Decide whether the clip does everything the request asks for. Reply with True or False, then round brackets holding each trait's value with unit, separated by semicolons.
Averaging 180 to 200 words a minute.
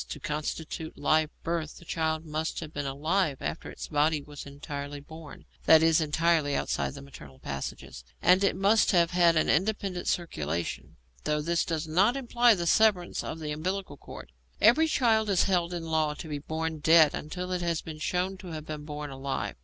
True (190 wpm)